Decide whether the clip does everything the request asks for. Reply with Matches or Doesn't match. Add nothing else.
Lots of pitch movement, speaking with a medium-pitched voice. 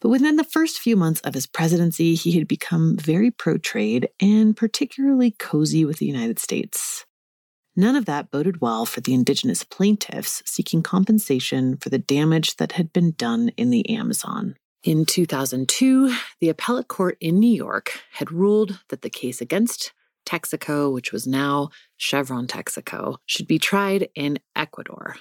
Matches